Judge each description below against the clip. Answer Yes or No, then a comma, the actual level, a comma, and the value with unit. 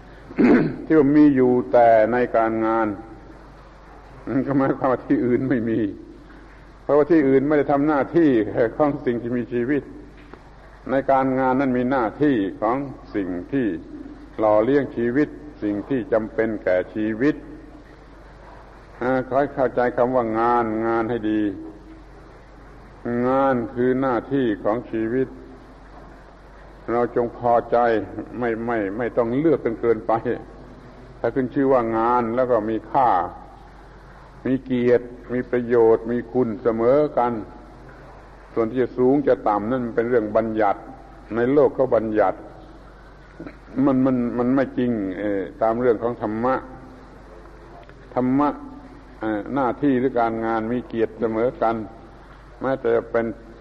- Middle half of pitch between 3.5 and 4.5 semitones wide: No, average, 2.7 semitones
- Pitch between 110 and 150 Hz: Yes, low, 120 Hz